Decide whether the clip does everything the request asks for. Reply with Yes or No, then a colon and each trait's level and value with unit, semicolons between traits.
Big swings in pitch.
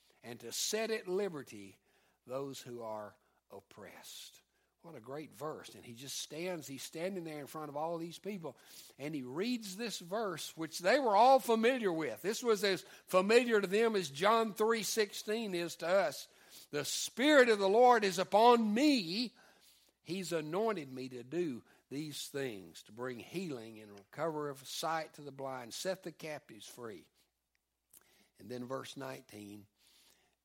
Yes: wide, 8.1 semitones